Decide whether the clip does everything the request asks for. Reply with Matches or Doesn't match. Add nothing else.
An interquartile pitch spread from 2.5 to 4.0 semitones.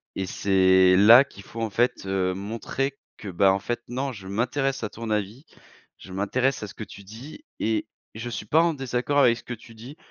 Doesn't match